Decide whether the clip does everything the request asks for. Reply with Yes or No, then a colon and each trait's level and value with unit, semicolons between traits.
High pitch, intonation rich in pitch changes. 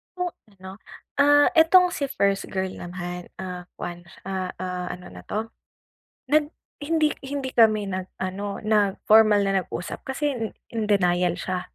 Yes: high, 200 Hz; wide, 6.4 semitones